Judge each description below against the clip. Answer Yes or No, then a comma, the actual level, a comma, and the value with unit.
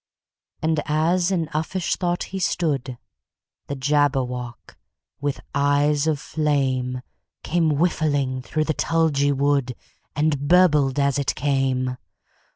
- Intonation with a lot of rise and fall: No, average, 2.8 semitones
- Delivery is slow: Yes, slow, 100 wpm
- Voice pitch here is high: No, medium, 145 Hz